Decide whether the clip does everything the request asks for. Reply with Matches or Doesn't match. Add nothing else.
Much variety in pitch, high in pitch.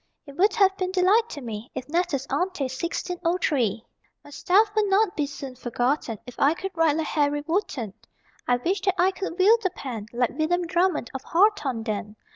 Matches